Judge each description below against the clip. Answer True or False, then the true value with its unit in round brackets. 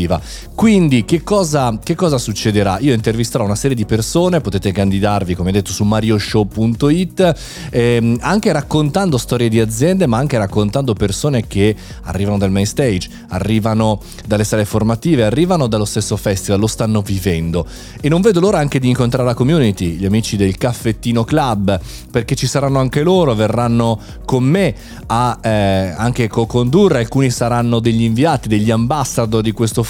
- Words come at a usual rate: True (160 wpm)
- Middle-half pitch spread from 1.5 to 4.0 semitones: False (4.7 semitones)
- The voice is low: True (115 Hz)